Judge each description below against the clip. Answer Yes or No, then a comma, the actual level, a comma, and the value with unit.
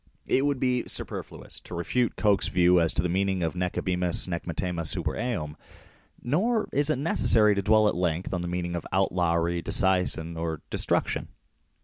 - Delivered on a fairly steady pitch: No, average, 4.1 semitones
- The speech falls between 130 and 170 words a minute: No, average, 180 wpm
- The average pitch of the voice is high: No, very low, 90 Hz